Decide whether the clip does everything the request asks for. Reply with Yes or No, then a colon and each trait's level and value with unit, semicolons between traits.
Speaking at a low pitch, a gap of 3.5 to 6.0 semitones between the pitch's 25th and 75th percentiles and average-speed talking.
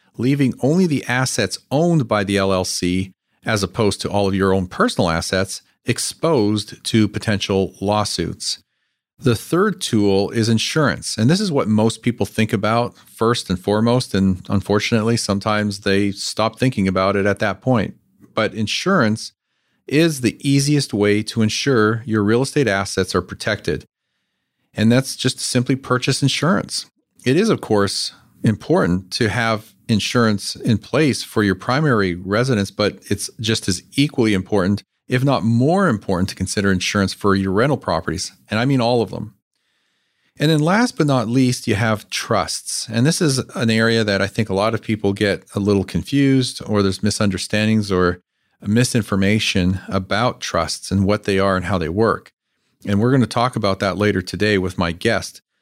Yes: low, 105 Hz; average, 3.8 semitones; average, 170 wpm